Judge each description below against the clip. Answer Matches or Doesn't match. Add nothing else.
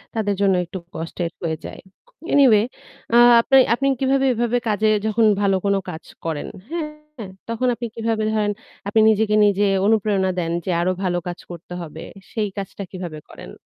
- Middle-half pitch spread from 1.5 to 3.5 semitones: Doesn't match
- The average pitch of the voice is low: Doesn't match